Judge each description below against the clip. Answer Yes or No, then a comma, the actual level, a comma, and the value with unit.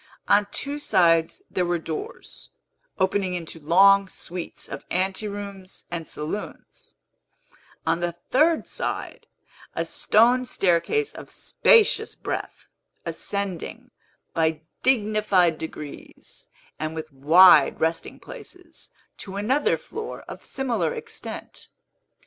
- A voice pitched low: No, high, 190 Hz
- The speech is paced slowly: Yes, slow, 105 wpm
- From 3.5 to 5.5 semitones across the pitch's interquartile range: Yes, average, 4.5 semitones